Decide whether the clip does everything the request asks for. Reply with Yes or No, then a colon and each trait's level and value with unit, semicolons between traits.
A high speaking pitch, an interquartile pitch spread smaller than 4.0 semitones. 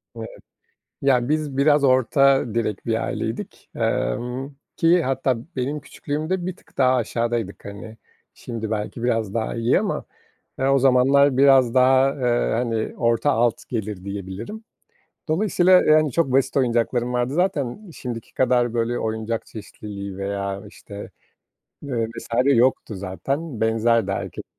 No: low, 125 Hz; average, 3.5 semitones